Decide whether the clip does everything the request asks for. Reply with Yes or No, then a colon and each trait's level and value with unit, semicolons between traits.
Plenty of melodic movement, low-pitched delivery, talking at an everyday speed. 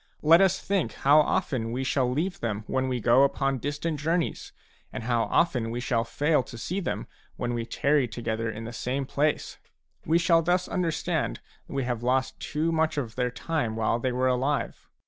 No: average, 4.6 semitones; low, 130 Hz; average, 195 wpm